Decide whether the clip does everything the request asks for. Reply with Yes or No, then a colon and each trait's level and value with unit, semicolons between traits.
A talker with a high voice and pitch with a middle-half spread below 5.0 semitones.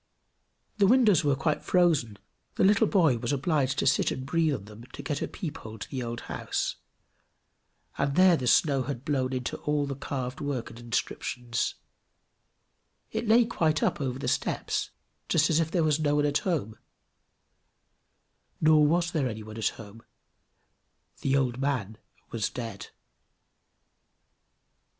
No: medium, 140 Hz; average, 4.6 semitones